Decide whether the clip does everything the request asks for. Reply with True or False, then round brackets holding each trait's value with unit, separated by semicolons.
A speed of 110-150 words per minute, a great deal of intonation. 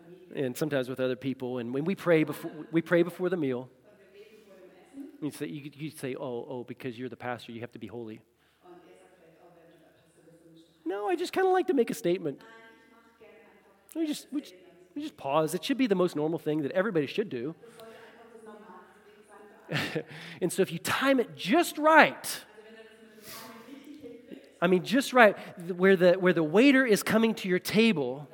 False (165 wpm; 6.5 semitones)